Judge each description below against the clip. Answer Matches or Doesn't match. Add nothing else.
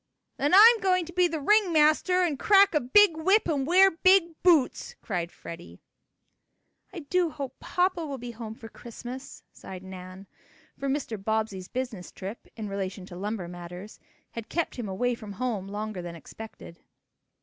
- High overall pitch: Matches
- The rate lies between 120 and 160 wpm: Doesn't match